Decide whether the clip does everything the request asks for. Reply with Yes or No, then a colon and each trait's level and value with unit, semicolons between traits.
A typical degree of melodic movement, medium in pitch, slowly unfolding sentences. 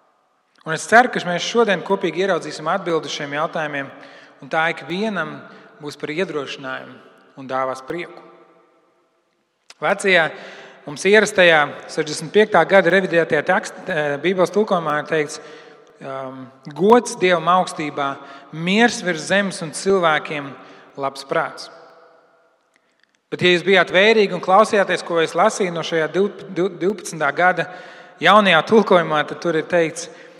Yes: average, 3.9 semitones; medium, 170 Hz; slow, 120 wpm